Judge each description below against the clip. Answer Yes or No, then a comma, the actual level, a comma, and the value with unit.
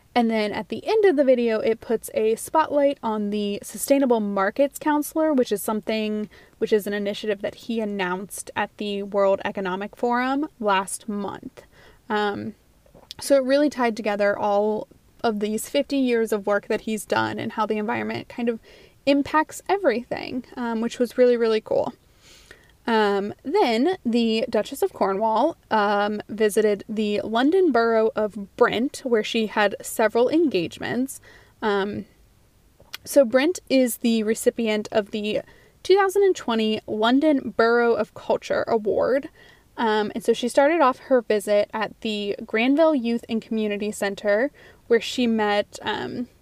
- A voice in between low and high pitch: No, high, 225 Hz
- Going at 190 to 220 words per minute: No, average, 150 wpm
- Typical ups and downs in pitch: Yes, average, 4.0 semitones